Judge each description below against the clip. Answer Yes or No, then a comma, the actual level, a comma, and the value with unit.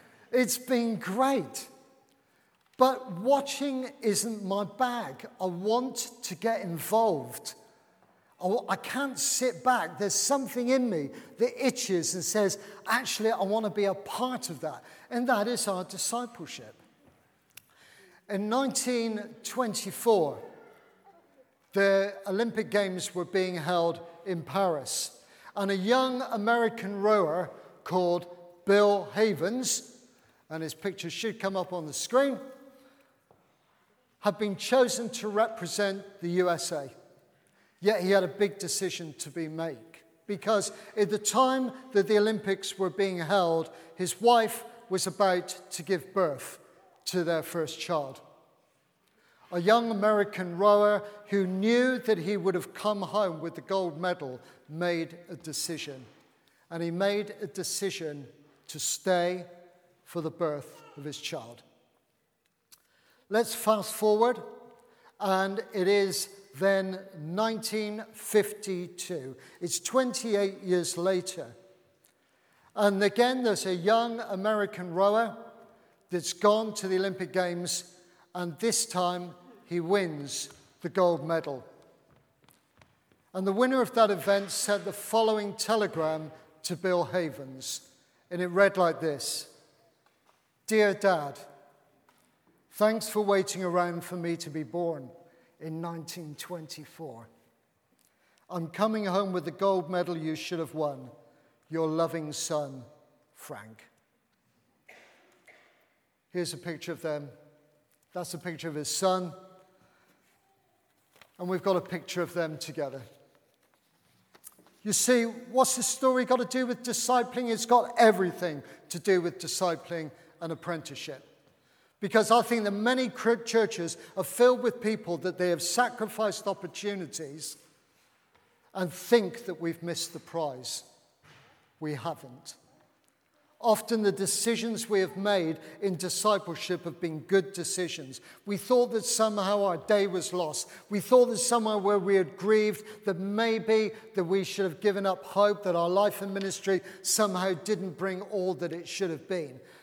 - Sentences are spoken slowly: Yes, slow, 130 wpm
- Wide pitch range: No, average, 4.2 semitones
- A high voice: Yes, high, 195 Hz